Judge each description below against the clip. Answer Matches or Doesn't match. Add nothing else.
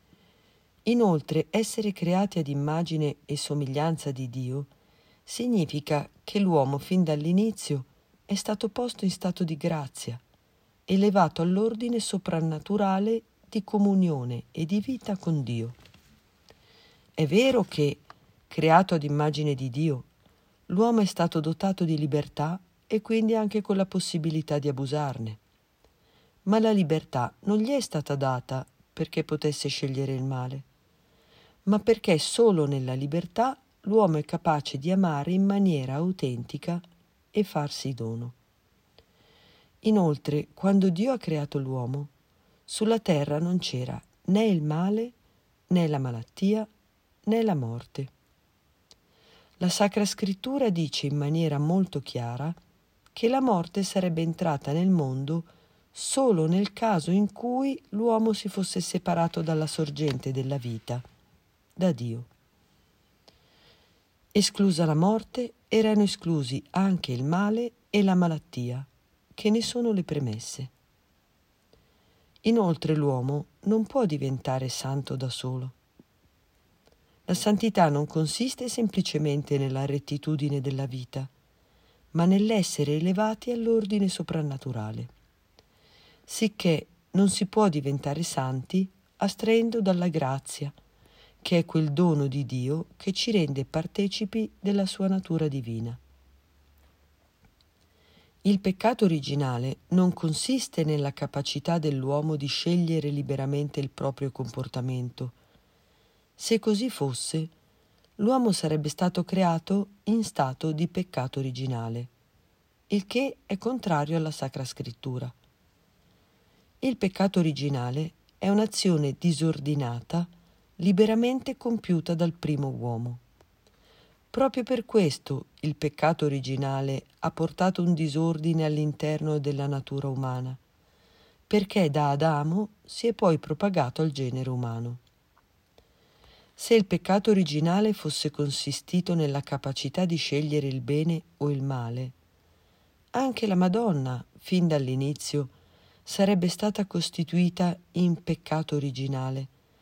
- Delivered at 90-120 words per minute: Matches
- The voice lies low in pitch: Doesn't match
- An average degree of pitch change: Doesn't match